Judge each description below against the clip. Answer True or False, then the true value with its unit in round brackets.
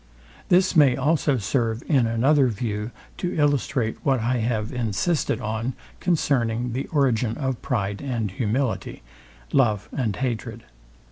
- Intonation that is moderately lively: True (3.8 semitones)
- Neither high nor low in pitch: False (125 Hz)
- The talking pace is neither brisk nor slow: False (130 wpm)